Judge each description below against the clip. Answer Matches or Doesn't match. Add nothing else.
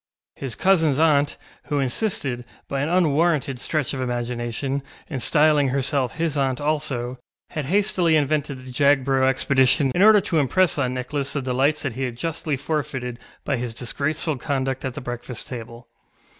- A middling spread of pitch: Matches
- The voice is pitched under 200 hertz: Matches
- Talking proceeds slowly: Doesn't match